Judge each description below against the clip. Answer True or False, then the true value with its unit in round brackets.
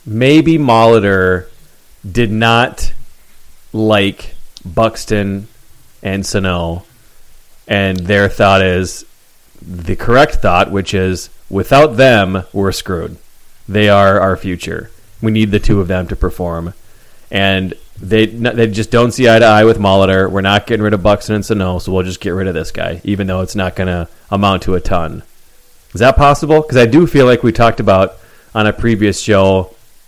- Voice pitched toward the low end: True (100 Hz)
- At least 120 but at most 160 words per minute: False (170 wpm)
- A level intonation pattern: False (3.3 semitones)